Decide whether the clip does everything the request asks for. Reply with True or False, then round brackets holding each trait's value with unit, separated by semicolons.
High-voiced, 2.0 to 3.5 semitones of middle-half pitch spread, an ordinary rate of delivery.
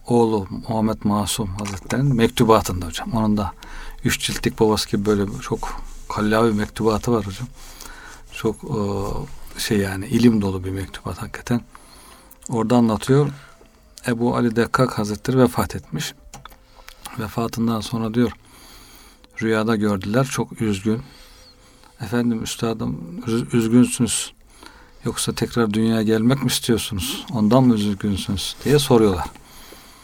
False (115 Hz; 2.4 semitones; 110 wpm)